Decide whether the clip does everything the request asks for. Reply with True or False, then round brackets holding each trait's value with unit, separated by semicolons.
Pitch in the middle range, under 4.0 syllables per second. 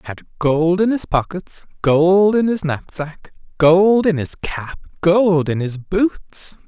True (170 Hz; 3.5 syllables/s)